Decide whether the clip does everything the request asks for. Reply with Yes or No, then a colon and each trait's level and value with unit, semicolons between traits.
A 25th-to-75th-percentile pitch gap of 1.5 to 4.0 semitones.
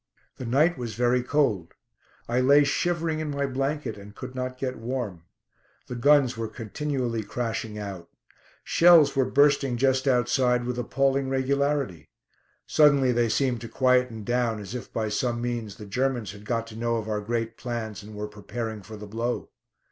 Yes: average, 3.4 semitones